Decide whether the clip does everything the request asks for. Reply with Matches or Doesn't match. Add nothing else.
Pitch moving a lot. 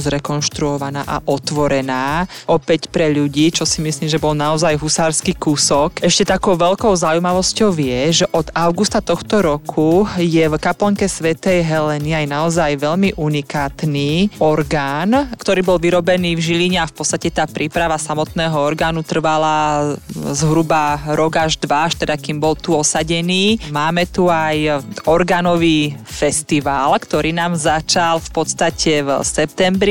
Doesn't match